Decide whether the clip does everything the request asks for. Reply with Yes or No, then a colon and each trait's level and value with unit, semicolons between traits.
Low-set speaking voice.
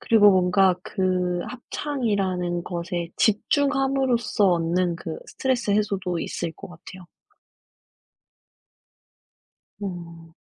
No: medium, 185 Hz